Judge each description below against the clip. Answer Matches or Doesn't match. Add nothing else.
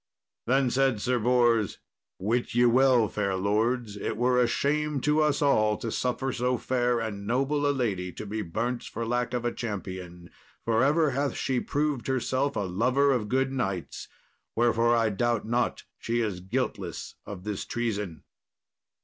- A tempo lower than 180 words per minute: Matches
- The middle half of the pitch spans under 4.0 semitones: Matches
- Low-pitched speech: Matches